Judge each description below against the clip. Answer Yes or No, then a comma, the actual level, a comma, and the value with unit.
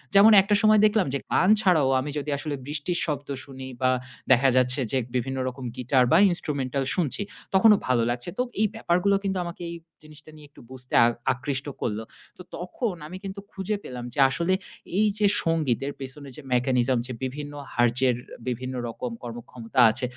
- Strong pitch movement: Yes, wide, 5.9 semitones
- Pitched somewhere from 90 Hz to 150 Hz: Yes, medium, 140 Hz